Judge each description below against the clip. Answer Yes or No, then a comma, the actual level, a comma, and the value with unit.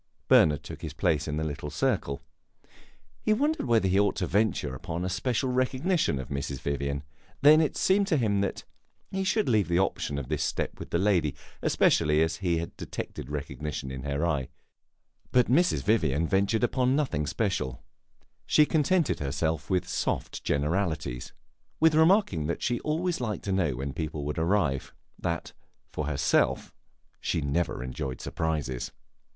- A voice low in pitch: Yes, very low, 85 Hz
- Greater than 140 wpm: Yes, average, 165 wpm